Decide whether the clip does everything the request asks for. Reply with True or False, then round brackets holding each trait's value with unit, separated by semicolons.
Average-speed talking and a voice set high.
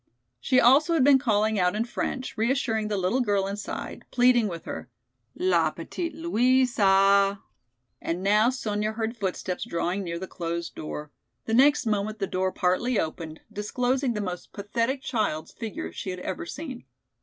True (160 wpm; 210 Hz)